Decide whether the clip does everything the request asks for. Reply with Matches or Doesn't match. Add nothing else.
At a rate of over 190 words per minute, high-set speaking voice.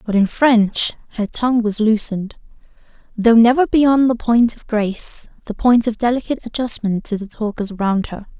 Doesn't match